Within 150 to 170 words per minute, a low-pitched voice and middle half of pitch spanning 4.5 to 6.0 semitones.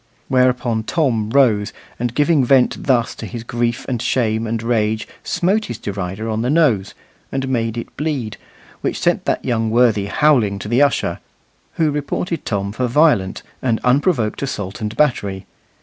No: average, 165 wpm; low, 120 Hz; average, 3.8 semitones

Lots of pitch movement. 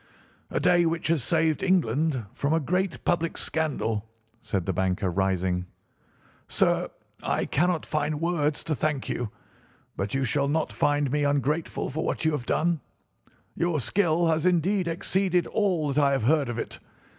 No: average, 4.4 semitones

